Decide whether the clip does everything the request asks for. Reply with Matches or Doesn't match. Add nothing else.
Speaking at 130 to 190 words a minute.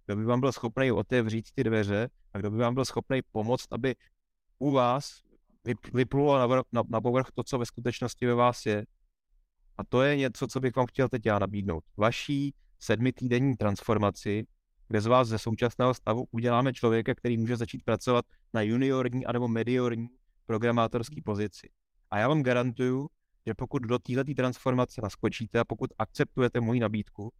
Matches